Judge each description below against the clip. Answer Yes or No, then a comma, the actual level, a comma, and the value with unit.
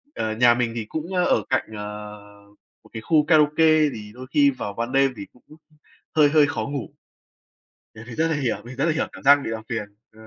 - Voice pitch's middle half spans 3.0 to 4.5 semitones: No, average, 5.2 semitones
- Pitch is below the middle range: Yes, low, 130 Hz